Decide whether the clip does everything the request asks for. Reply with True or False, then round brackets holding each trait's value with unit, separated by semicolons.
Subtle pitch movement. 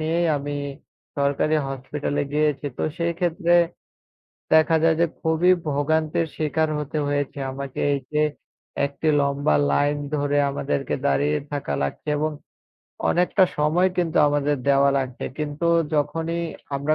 True (2.2 semitones)